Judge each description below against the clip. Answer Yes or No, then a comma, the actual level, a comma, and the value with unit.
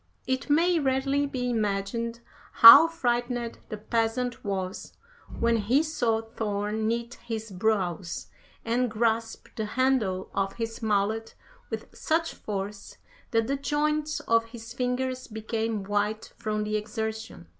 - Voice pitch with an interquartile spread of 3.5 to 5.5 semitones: No, average, 2.8 semitones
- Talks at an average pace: No, slow, 130 wpm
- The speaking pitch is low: No, high, 225 Hz